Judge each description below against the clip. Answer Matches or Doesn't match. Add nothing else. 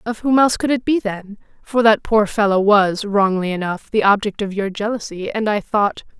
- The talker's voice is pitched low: Doesn't match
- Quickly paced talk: Matches